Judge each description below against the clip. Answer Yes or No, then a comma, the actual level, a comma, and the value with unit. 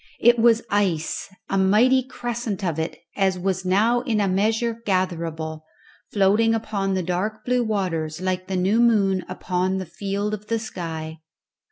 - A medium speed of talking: Yes, average, 160 wpm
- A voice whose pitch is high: Yes, high, 195 Hz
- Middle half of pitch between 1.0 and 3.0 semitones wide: No, average, 3.4 semitones